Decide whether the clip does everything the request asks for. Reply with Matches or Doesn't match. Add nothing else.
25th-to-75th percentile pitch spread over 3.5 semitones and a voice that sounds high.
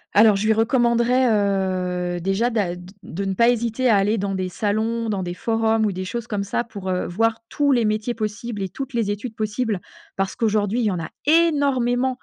Doesn't match